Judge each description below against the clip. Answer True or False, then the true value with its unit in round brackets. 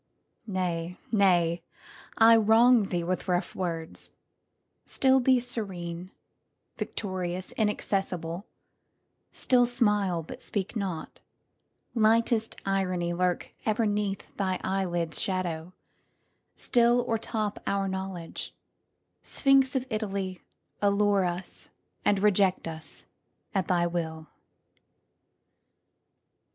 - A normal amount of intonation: True (3.7 semitones)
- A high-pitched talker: True (195 Hz)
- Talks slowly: True (80 wpm)